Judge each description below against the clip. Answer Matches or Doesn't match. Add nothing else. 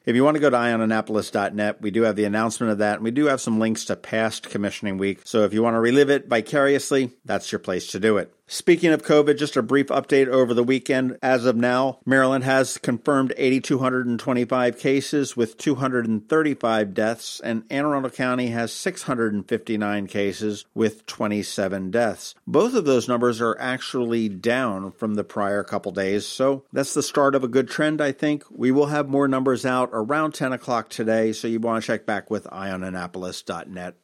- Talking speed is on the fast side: Doesn't match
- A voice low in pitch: Matches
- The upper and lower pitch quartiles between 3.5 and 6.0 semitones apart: Matches